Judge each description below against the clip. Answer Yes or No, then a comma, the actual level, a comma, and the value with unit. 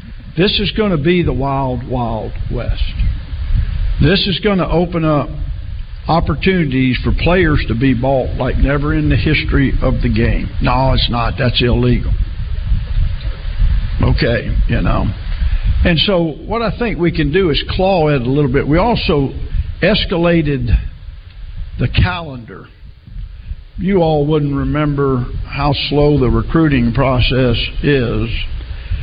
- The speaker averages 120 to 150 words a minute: Yes, average, 140 wpm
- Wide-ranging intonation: Yes, wide, 7.9 semitones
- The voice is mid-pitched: No, low, 125 Hz